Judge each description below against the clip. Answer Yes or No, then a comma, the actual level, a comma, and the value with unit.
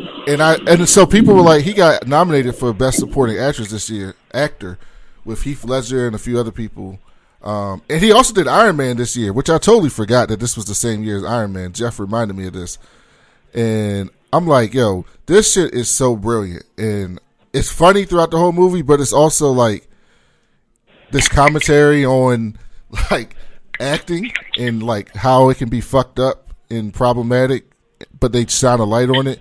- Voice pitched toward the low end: Yes, low, 125 Hz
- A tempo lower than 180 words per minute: No, average, 190 wpm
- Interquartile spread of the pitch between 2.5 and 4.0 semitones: No, average, 4.9 semitones